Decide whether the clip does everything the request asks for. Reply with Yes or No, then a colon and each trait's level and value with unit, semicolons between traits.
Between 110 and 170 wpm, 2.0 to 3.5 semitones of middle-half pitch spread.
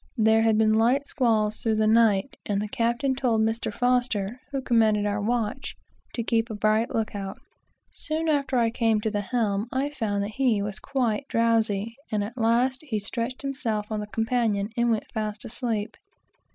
No: average, 185 wpm; narrow, 2.5 semitones